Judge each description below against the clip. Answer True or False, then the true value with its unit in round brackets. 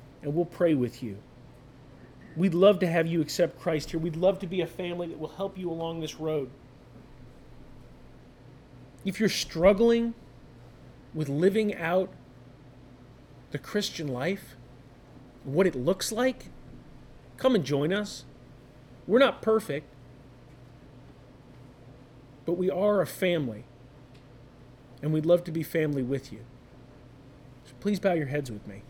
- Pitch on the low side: False (145 Hz)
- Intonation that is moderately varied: False (5.9 semitones)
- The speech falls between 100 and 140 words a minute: True (135 wpm)